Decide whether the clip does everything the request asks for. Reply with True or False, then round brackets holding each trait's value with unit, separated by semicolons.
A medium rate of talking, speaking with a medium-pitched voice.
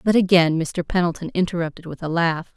True (190 wpm; 170 Hz)